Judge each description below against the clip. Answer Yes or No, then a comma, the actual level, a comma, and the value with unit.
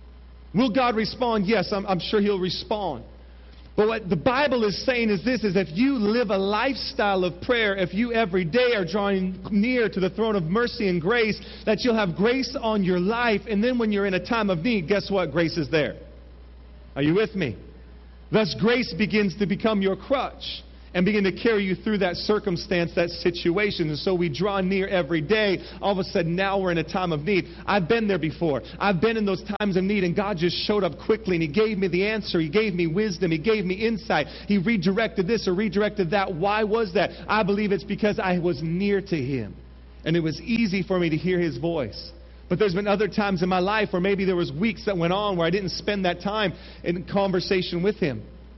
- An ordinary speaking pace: No, fast, 225 wpm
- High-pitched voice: Yes, high, 195 Hz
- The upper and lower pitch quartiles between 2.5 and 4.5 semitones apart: Yes, average, 3.4 semitones